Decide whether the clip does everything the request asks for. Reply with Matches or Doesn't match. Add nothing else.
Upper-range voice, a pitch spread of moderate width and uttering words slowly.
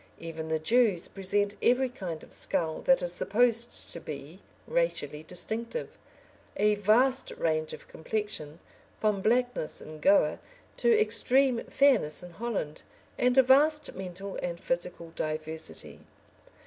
Doesn't match